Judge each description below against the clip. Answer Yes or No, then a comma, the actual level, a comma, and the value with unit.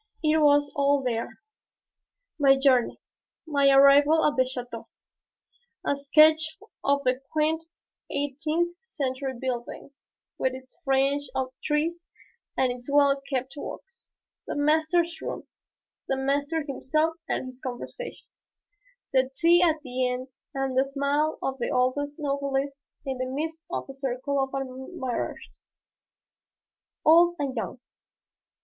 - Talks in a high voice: Yes, very high, 280 Hz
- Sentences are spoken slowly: Yes, slow, 130 wpm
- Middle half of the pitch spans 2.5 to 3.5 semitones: Yes, average, 2.8 semitones